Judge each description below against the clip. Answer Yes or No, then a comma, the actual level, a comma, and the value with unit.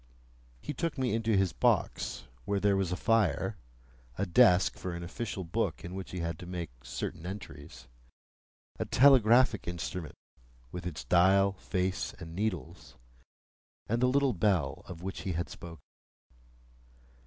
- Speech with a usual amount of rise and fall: Yes, average, 3.9 semitones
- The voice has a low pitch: Yes, very low, 95 Hz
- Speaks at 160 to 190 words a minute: No, average, 150 wpm